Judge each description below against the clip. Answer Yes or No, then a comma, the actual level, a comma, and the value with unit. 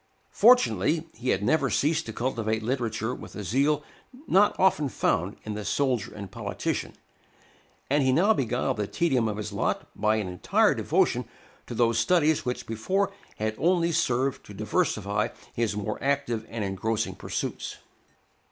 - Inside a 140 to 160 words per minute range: Yes, average, 155 wpm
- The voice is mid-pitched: No, low, 120 Hz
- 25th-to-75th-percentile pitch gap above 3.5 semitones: Yes, wide, 5.6 semitones